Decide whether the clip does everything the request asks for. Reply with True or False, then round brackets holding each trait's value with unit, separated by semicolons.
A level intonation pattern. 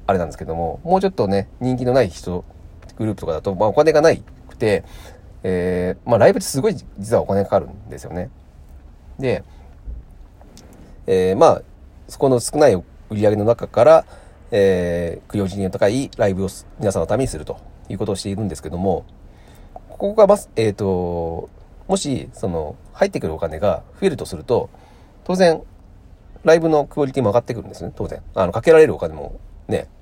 False (5.6 semitones)